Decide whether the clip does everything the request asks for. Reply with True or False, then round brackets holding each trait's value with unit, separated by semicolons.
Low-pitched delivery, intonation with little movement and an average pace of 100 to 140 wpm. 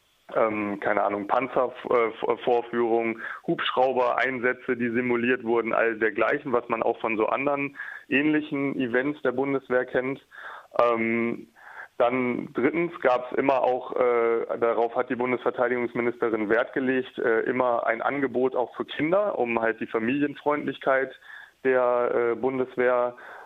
True (125 Hz; 1.9 semitones; 130 wpm)